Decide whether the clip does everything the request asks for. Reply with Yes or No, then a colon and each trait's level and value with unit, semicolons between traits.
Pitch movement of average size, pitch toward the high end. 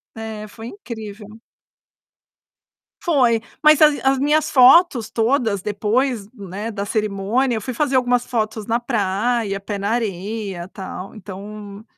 Yes: average, 3.4 semitones; high, 220 Hz